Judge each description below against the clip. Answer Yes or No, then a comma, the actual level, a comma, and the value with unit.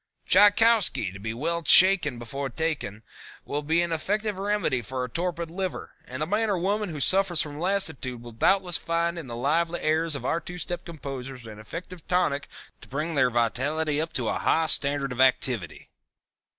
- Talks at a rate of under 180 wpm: No, average, 185 wpm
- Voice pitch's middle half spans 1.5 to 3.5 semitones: No, average, 5.3 semitones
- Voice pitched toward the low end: No, medium, 160 Hz